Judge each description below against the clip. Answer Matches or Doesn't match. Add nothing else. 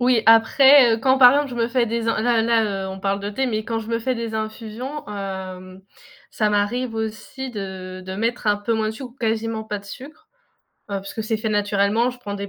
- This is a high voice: Matches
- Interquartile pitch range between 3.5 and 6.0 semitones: Doesn't match